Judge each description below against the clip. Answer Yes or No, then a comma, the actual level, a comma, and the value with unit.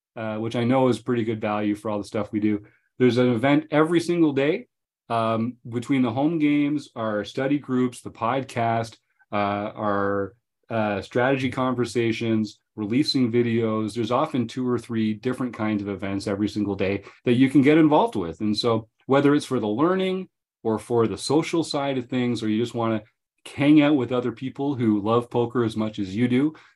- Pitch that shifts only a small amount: No, average, 3.7 semitones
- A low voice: Yes, low, 120 Hz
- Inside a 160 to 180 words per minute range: No, average, 195 wpm